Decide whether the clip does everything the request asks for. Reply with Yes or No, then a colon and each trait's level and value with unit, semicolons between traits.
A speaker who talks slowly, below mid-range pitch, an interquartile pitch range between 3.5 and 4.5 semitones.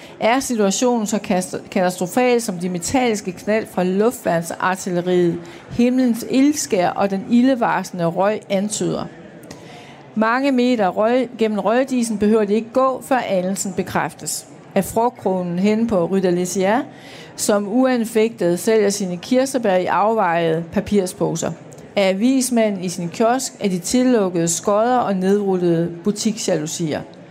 No: slow, 120 wpm; high, 205 Hz; average, 4.2 semitones